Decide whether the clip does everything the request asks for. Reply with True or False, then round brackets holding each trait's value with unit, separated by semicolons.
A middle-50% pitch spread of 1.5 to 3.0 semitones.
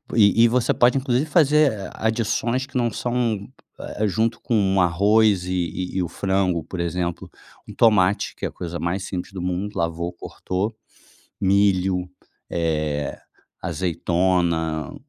False (4.2 semitones)